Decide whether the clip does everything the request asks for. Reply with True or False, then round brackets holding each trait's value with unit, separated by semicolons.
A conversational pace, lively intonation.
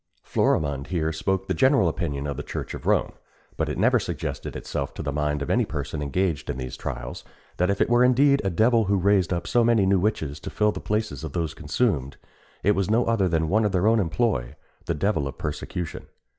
False (225 wpm; 6.3 semitones)